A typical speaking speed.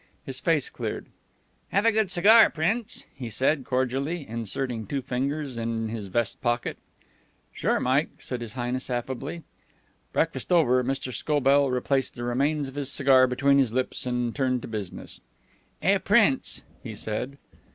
Yes: average, 150 wpm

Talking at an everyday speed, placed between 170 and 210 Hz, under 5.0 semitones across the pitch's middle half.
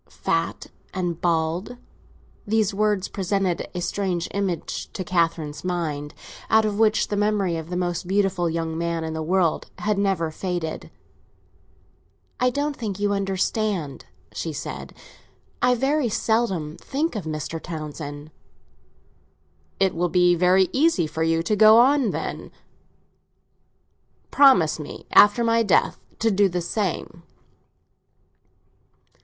No: slow, 130 wpm; medium, 185 Hz; average, 4.3 semitones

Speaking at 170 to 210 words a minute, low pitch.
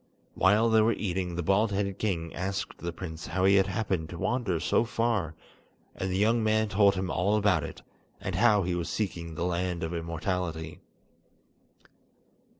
Yes: average, 175 wpm; very low, 95 Hz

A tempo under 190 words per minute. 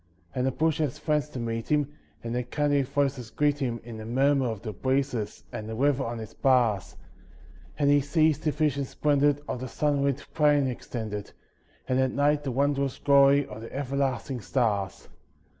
Yes: average, 180 wpm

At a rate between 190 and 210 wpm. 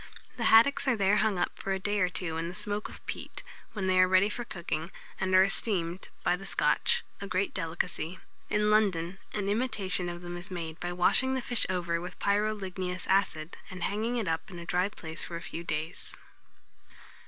Yes: fast, 205 wpm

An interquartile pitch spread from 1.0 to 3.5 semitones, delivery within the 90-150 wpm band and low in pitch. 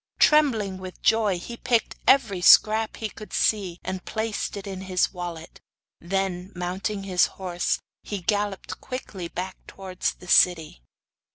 No: average, 2.9 semitones; average, 145 wpm; high, 190 Hz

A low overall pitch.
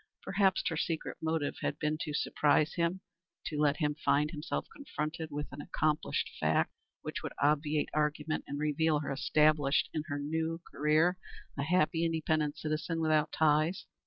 No: medium, 155 Hz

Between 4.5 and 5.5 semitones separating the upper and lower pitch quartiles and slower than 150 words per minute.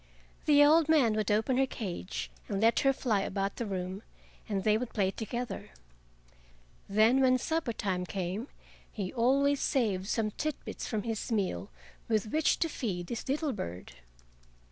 No: average, 5.1 semitones; average, 165 wpm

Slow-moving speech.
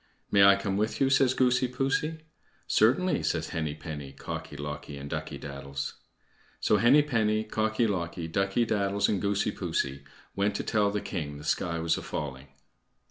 No: average, 170 wpm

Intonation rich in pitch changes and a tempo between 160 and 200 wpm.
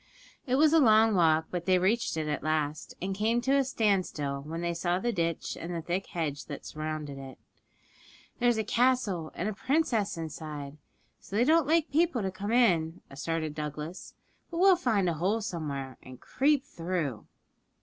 Yes: wide, 7.2 semitones; average, 180 wpm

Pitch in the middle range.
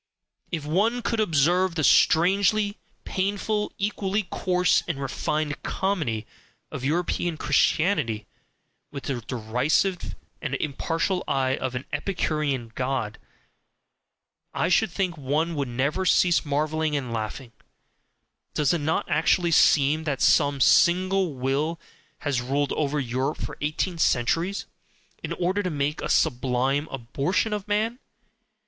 Yes: medium, 155 Hz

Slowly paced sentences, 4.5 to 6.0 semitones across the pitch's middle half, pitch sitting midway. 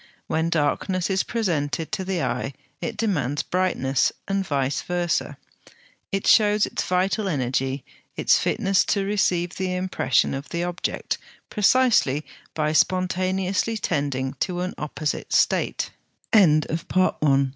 Yes: slow, 120 wpm; average, 4.8 semitones; medium, 180 Hz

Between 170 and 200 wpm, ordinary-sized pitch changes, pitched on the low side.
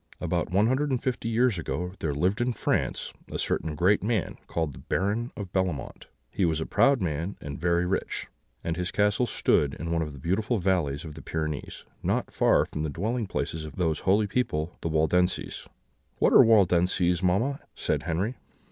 Yes: average, 190 wpm; average, 4.7 semitones; very low, 90 Hz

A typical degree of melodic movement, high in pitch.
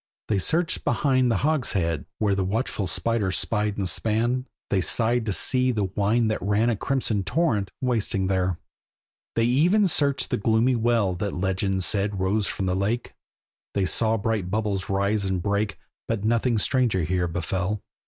No: average, 3.6 semitones; low, 105 Hz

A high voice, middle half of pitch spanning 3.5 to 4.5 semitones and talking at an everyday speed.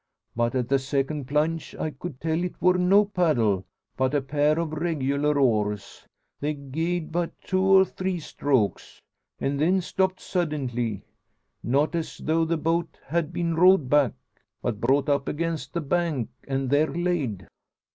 No: medium, 150 Hz; average, 4.1 semitones; average, 155 wpm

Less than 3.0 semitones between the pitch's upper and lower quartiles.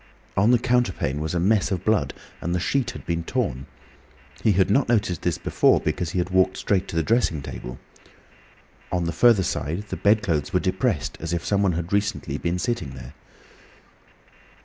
No: average, 4.3 semitones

